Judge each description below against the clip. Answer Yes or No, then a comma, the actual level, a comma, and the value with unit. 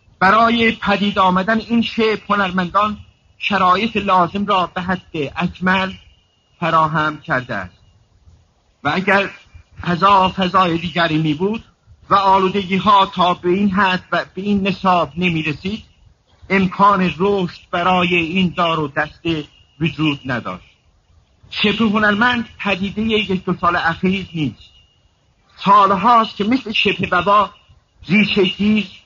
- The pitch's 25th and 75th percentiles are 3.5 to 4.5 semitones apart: Yes, average, 3.9 semitones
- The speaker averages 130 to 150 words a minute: No, average, 120 wpm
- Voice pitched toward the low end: No, medium, 185 Hz